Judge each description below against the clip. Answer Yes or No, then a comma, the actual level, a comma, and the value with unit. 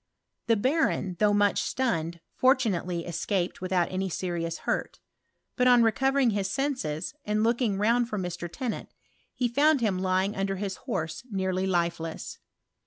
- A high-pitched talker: Yes, high, 195 Hz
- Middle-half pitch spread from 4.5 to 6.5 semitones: Yes, average, 5.0 semitones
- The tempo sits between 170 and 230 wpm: No, average, 140 wpm